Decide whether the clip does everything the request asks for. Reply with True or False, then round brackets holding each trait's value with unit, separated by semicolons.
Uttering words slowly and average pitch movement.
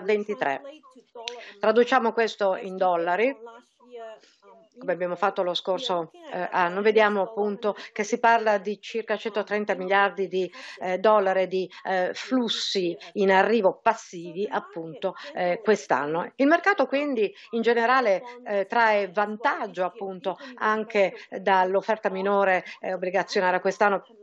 True (120 wpm; 3.4 semitones)